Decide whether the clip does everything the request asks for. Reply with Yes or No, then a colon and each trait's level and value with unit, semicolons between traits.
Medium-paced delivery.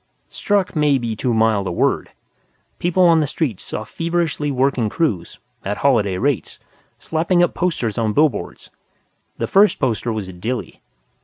Yes: average, 155 wpm